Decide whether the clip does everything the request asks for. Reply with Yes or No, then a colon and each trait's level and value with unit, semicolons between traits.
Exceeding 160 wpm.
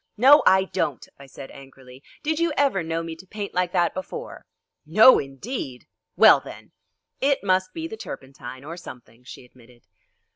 Yes: average, 170 wpm